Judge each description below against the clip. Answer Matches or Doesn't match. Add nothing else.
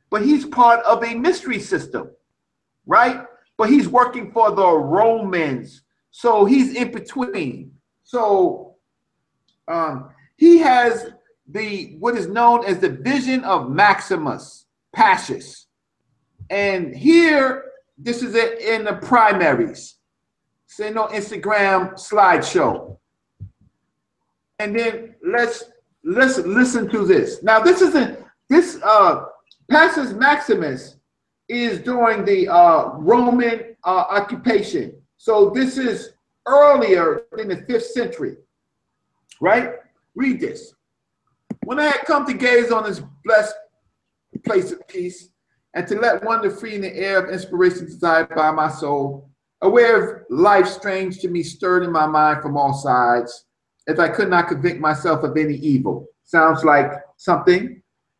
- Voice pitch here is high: Matches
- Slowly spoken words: Matches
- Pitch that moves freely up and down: Matches